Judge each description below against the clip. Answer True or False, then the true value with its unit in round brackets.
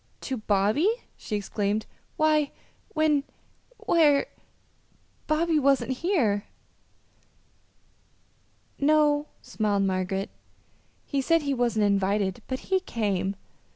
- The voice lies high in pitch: True (260 Hz)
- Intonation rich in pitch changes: True (7.0 semitones)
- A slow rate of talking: True (90 wpm)